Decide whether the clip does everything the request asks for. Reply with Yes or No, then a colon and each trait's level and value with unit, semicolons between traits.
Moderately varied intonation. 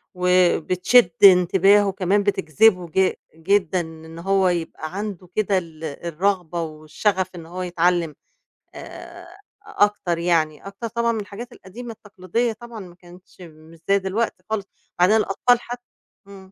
Yes: average, 3.1 semitones